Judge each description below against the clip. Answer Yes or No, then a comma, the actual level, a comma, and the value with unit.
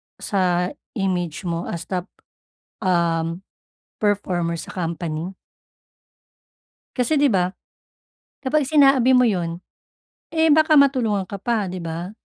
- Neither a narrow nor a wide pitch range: No, wide, 6.5 semitones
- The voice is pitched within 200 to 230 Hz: No, high, 190 Hz